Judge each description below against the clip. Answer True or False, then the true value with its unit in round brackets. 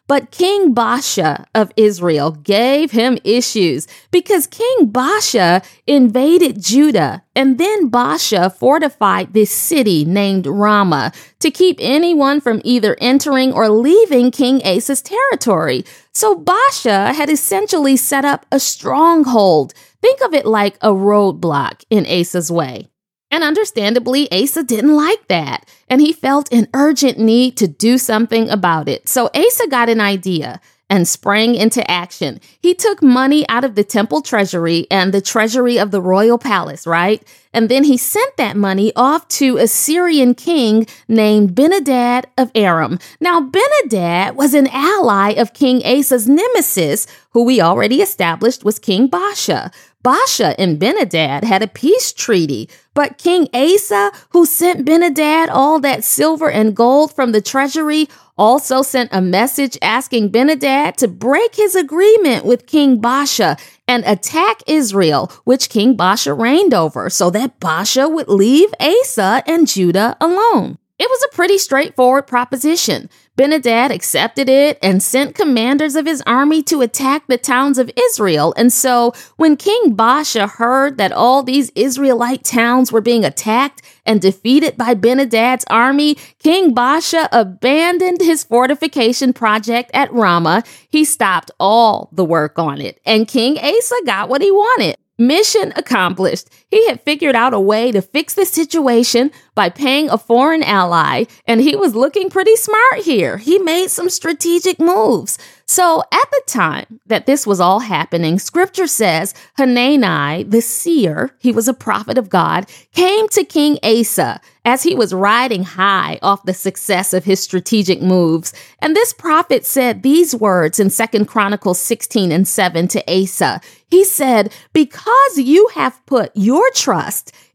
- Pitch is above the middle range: True (250 Hz)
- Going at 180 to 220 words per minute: False (150 wpm)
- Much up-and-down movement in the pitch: True (6.3 semitones)